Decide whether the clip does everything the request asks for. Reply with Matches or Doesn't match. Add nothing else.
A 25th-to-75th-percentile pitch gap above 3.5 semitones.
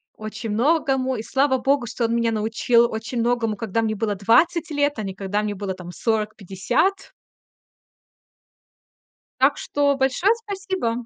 Matches